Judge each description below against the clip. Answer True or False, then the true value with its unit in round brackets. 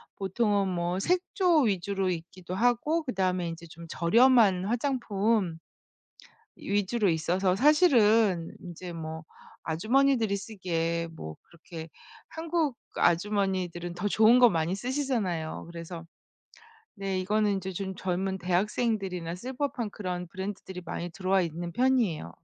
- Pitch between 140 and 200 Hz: True (190 Hz)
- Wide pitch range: False (4.8 semitones)